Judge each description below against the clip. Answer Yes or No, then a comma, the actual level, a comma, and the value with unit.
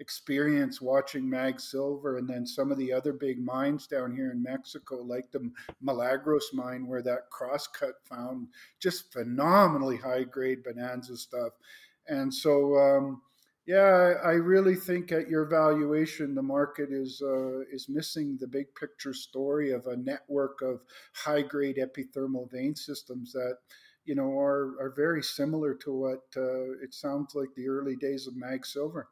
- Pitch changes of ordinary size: No, narrow, 2.1 semitones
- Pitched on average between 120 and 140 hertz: Yes, low, 135 Hz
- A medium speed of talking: Yes, average, 155 wpm